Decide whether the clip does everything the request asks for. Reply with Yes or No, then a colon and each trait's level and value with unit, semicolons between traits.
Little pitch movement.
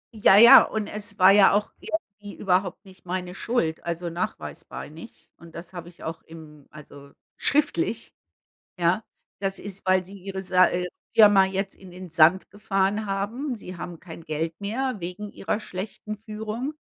No: average, 3.2 semitones